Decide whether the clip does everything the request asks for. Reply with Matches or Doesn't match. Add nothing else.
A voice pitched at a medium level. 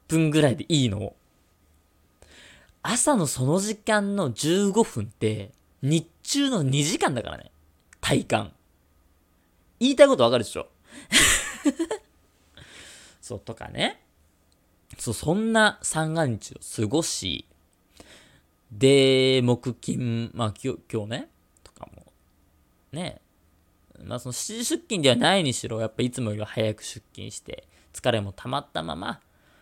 Doesn't match